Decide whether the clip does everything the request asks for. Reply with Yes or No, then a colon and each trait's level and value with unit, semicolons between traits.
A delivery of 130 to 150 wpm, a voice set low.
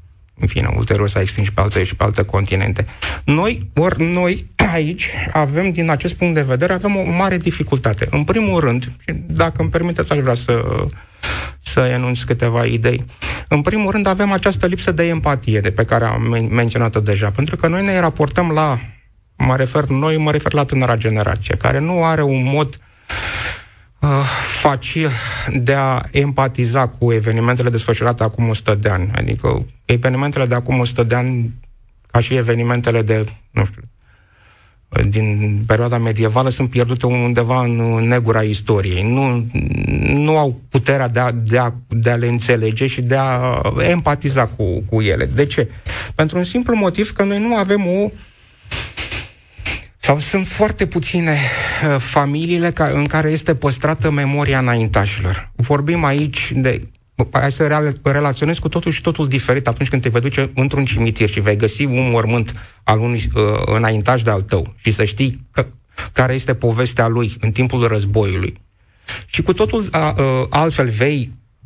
No: average, 165 wpm; low, 125 Hz